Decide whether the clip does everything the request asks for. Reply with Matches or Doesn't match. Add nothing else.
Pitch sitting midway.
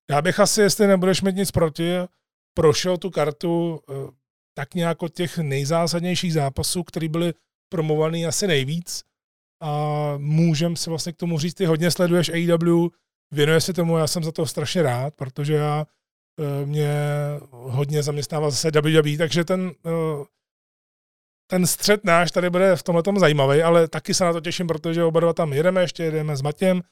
Matches